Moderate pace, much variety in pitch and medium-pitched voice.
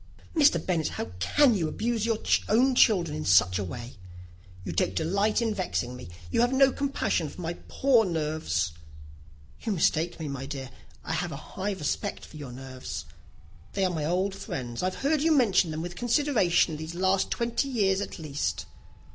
Yes: average, 180 wpm; wide, 7.6 semitones; medium, 175 Hz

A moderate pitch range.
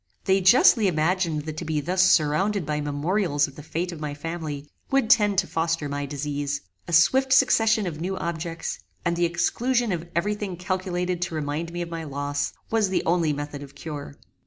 Yes: average, 4.0 semitones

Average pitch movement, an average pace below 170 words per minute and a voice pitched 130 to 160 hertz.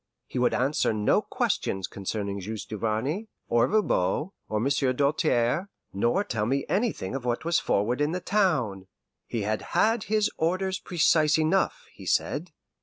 No: wide, 8.9 semitones; average, 155 wpm; low, 135 Hz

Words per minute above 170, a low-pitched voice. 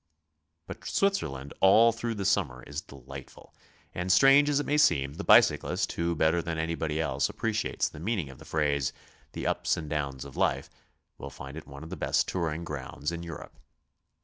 Yes: average, 185 wpm; very low, 80 Hz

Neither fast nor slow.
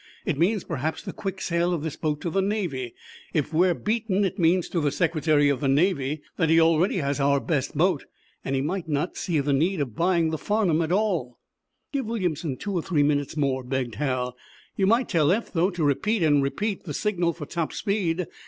No: fast, 215 wpm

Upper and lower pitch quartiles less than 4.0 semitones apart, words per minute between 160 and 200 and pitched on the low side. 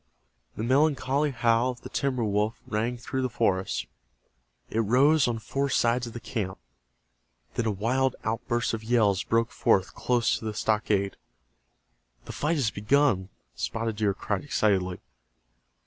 No: average, 3.2 semitones; average, 145 wpm; low, 115 Hz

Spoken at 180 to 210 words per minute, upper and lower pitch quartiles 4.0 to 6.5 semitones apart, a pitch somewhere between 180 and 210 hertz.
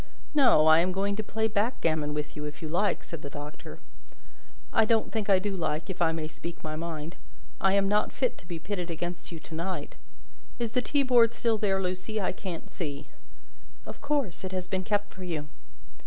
Yes: fast, 205 wpm; average, 4.6 semitones; medium, 185 Hz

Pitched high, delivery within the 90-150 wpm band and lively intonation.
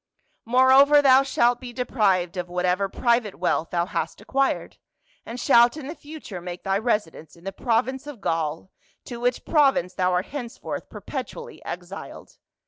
No: high, 230 Hz; average, 160 wpm; wide, 6.4 semitones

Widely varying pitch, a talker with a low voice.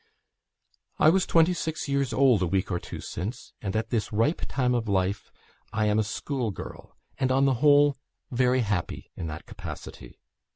No: average, 5.0 semitones; low, 120 Hz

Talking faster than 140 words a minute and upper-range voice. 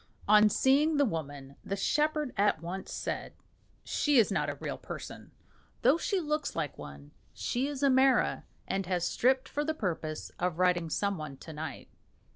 Yes: average, 175 wpm; high, 200 Hz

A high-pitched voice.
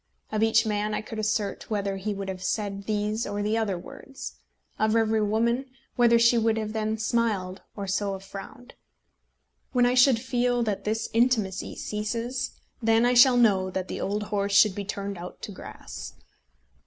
Yes: high, 215 Hz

